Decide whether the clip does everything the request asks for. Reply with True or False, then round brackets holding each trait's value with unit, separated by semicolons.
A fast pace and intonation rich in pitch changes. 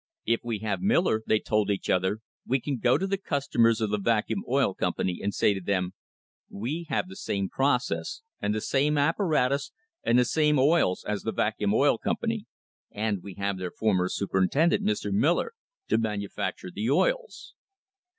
False (180 wpm; 6.1 semitones)